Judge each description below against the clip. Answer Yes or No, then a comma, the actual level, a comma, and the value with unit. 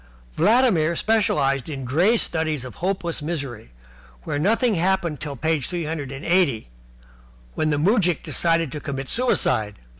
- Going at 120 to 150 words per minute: Yes, average, 145 wpm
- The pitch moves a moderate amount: Yes, average, 4.9 semitones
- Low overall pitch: No, medium, 160 Hz